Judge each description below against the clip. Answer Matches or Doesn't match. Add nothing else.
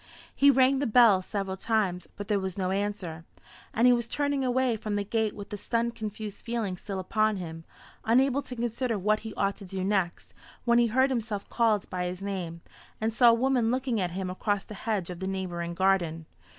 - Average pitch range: Matches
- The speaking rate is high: Matches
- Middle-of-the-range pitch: Doesn't match